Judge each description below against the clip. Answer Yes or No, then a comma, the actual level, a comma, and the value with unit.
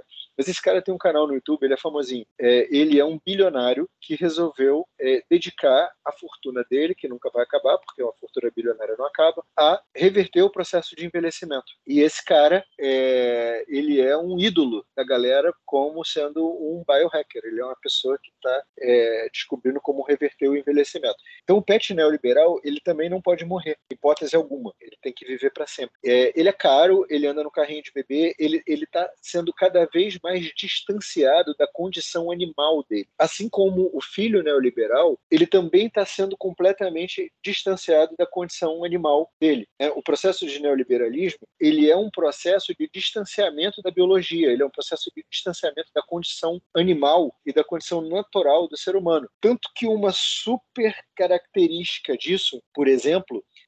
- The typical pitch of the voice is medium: Yes, medium, 175 Hz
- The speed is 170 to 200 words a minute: Yes, average, 175 wpm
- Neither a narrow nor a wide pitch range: No, wide, 5.9 semitones